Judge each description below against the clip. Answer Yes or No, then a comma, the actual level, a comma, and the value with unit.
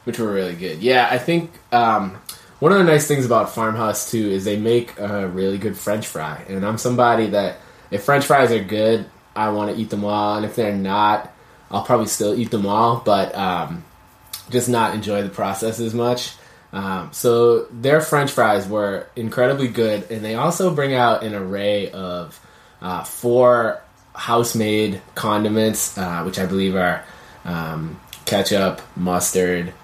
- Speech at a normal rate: Yes, average, 175 wpm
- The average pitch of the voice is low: Yes, low, 110 Hz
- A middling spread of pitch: Yes, average, 3.4 semitones